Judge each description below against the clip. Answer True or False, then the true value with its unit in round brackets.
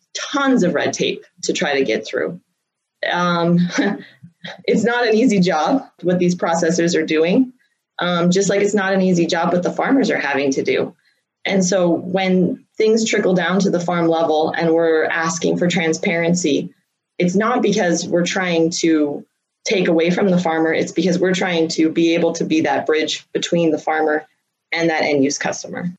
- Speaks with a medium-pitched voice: True (175 Hz)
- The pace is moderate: True (185 wpm)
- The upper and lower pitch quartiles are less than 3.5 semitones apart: True (2.8 semitones)